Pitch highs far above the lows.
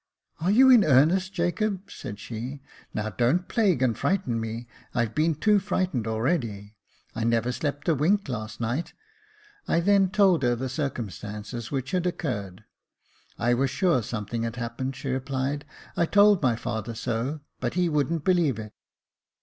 Yes: wide, 7.1 semitones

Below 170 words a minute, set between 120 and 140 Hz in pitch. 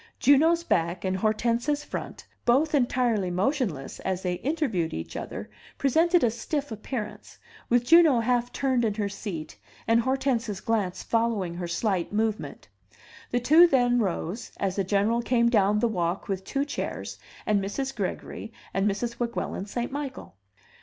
No: average, 155 wpm; high, 230 Hz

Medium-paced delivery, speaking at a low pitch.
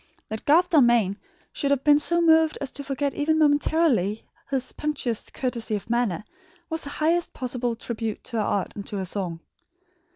No: average, 175 wpm; very high, 260 Hz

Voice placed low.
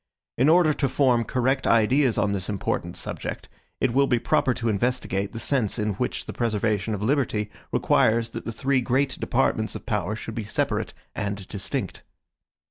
Yes: low, 115 Hz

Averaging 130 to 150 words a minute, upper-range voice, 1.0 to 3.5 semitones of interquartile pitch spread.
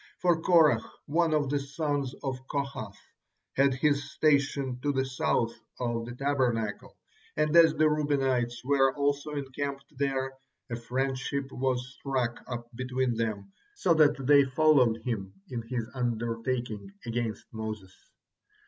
No: slow, 135 wpm; low, 130 Hz; average, 3.2 semitones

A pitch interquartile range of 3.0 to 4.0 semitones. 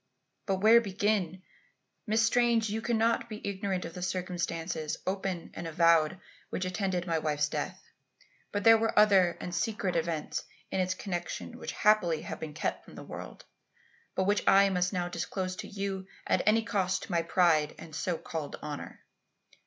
Yes: average, 3.5 semitones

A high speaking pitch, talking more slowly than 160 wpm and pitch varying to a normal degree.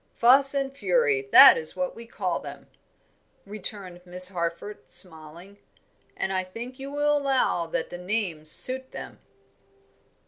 No: high, 210 Hz; average, 140 wpm; wide, 7.2 semitones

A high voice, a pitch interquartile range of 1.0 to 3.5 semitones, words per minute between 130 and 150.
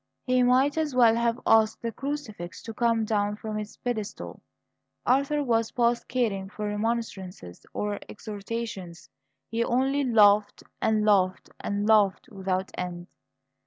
Yes: high, 220 Hz; average, 2.9 semitones; slow, 135 wpm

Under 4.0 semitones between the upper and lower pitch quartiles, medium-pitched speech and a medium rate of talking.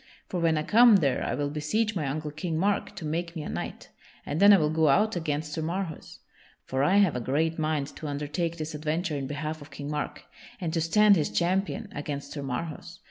No: average, 3.0 semitones; medium, 155 Hz; fast, 225 wpm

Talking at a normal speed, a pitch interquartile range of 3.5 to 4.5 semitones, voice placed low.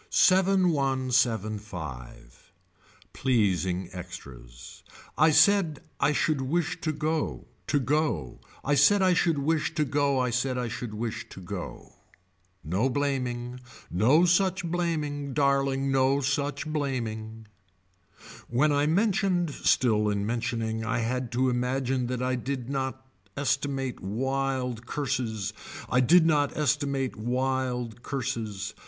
No: slow, 125 wpm; average, 4.1 semitones; low, 130 Hz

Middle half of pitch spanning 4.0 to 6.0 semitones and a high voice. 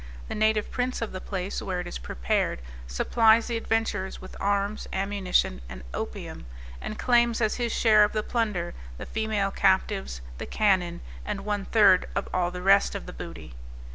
No: average, 3.2 semitones; high, 200 Hz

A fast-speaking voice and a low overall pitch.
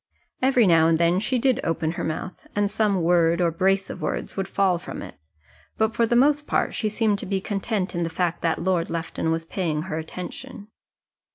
No: fast, 210 wpm; medium, 185 Hz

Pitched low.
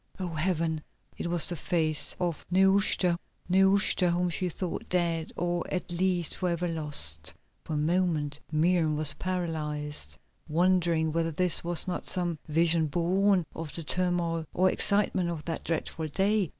No: medium, 170 Hz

